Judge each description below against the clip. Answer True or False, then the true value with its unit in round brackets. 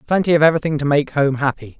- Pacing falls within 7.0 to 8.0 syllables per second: True (7.4 syllables/s)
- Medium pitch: True (150 Hz)